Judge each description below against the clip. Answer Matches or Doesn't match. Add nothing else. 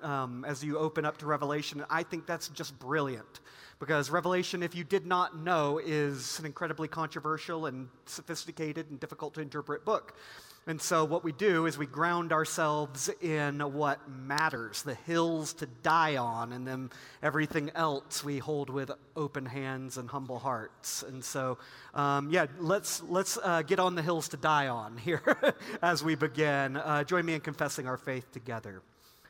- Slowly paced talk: Doesn't match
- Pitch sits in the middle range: Matches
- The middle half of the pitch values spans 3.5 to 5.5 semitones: Doesn't match